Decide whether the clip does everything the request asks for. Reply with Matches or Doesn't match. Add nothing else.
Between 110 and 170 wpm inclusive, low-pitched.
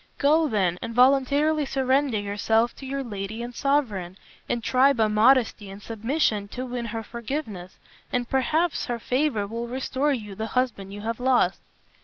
Doesn't match